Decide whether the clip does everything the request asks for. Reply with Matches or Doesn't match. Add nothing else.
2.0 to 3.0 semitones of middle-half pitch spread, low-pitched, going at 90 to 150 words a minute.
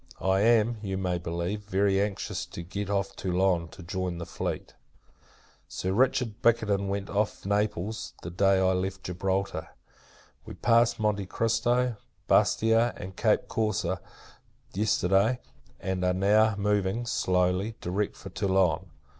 Matches